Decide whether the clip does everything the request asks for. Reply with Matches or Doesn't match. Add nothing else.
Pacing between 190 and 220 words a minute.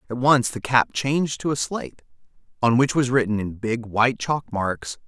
Matches